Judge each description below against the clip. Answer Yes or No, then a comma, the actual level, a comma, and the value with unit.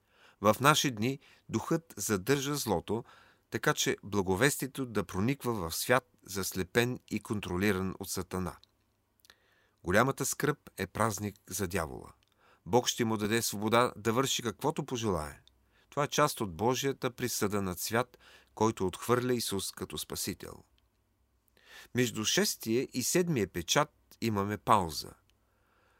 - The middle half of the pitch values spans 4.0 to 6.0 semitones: Yes, average, 4.8 semitones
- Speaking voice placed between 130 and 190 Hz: No, low, 110 Hz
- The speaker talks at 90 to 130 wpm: Yes, average, 120 wpm